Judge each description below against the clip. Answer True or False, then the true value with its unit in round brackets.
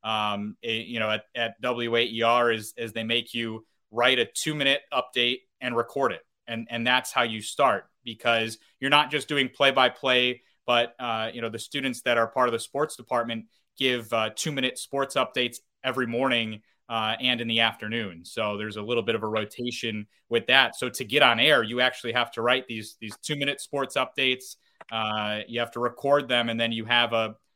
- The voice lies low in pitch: True (120 Hz)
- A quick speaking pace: True (210 wpm)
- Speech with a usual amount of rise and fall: False (2.2 semitones)